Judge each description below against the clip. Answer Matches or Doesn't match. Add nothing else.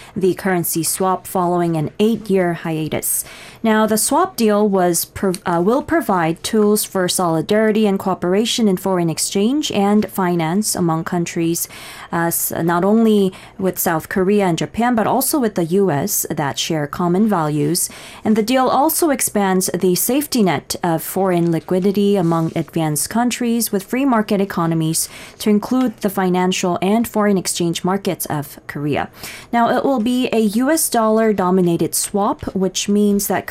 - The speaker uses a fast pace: Doesn't match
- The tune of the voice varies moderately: Matches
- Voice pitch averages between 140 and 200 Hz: Matches